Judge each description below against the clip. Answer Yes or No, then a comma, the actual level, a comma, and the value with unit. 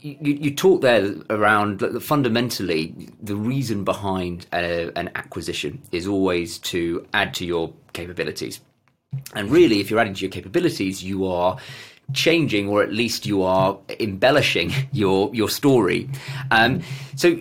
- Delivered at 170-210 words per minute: No, average, 145 wpm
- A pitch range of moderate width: No, wide, 6.3 semitones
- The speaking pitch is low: Yes, low, 105 Hz